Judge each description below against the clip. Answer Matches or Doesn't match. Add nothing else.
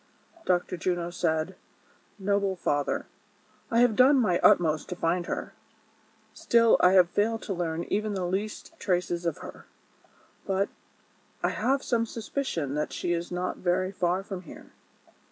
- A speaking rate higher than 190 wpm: Doesn't match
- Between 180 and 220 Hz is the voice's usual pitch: Matches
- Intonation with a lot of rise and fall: Doesn't match